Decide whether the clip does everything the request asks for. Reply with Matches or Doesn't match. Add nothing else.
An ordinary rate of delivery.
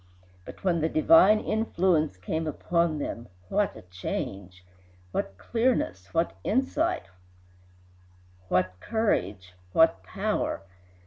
Doesn't match